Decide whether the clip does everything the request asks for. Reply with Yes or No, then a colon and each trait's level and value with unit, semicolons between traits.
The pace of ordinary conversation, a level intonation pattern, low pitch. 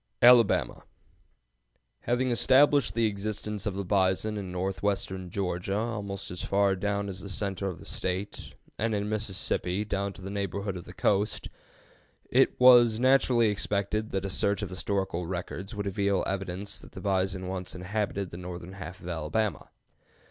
Yes: average, 160 wpm; narrow, 2.2 semitones; low, 100 Hz